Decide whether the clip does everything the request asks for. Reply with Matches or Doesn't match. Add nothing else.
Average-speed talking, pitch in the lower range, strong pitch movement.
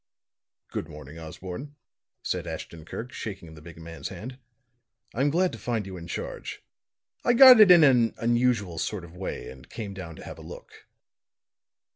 Matches